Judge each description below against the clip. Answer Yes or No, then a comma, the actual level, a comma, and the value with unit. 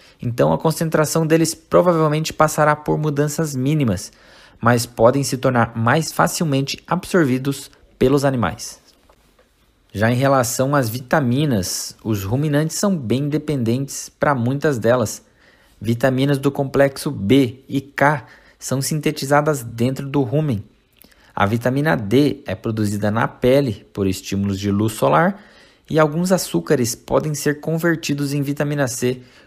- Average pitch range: Yes, average, 4.3 semitones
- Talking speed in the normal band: Yes, average, 130 wpm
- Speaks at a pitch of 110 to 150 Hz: Yes, low, 135 Hz